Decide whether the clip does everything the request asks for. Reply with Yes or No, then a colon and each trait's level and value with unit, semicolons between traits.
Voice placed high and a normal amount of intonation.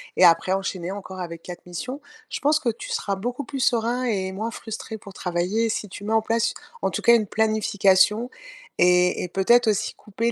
Yes: high, 210 Hz; average, 3.7 semitones